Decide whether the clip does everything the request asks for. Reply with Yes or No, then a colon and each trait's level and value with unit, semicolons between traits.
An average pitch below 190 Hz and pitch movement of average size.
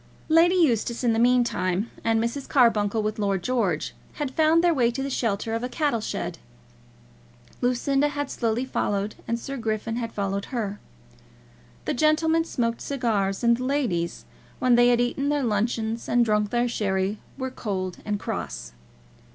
No: high, 235 Hz; average, 3.8 semitones